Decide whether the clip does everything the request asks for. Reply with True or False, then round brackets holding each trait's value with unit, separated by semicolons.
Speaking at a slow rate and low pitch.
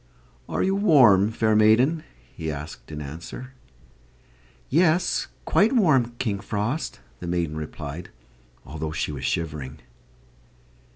True (115 wpm; 105 Hz)